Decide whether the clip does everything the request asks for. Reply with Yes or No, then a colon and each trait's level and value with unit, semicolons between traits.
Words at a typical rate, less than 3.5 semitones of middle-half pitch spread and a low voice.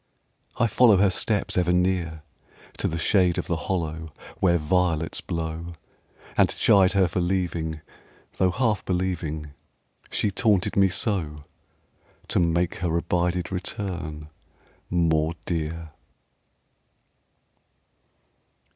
No: slow, 110 wpm; narrow, 2.6 semitones; very low, 90 Hz